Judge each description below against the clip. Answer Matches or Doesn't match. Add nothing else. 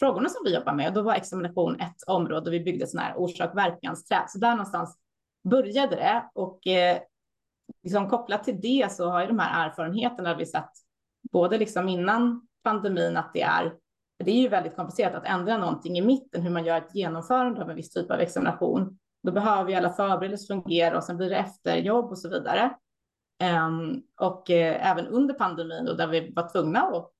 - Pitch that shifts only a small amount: Doesn't match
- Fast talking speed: Matches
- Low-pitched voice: Doesn't match